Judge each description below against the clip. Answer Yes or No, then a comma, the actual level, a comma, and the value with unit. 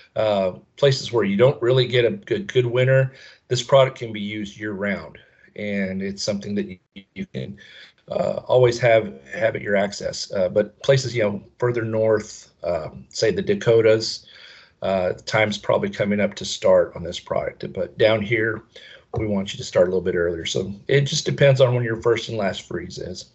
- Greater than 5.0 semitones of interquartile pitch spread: No, average, 3.5 semitones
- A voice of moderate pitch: No, low, 110 Hz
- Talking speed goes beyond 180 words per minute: Yes, average, 200 wpm